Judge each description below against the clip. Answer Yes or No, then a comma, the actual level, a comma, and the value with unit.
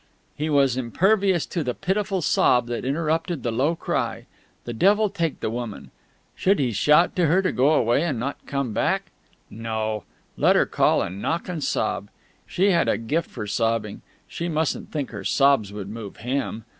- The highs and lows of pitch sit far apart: Yes, wide, 6.7 semitones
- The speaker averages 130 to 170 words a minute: No, average, 180 wpm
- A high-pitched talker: No, medium, 140 Hz